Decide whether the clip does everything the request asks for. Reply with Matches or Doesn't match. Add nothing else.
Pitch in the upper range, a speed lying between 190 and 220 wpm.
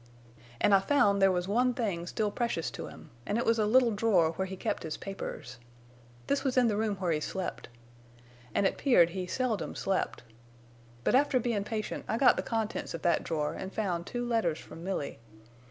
Matches